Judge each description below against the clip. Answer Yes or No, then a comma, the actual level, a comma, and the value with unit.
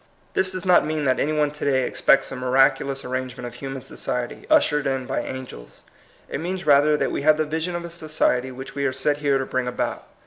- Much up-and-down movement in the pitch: No, average, 2.9 semitones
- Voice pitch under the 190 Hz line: Yes, medium, 140 Hz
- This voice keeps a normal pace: No, fast, 235 wpm